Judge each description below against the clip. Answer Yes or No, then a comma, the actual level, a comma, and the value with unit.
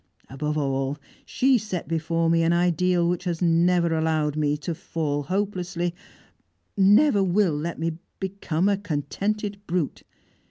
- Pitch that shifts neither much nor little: Yes, average, 3.4 semitones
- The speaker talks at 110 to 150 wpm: Yes, slow, 135 wpm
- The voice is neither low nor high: Yes, medium, 170 Hz